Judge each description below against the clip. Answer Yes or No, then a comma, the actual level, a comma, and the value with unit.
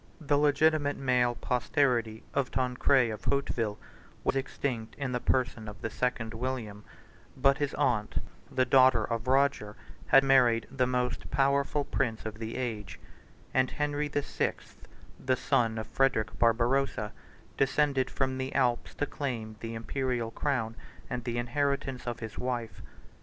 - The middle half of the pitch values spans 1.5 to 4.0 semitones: Yes, average, 3.1 semitones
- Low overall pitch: Yes, low, 125 Hz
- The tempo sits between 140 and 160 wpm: Yes, average, 145 wpm